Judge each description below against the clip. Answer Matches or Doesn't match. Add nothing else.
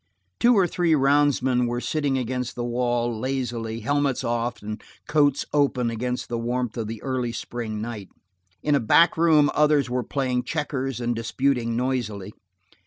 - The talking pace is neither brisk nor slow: Matches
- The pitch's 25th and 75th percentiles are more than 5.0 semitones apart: Doesn't match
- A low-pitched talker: Matches